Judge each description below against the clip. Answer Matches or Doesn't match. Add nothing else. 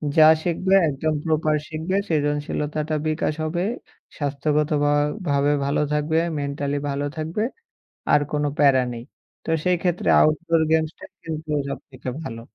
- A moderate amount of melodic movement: Doesn't match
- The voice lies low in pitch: Doesn't match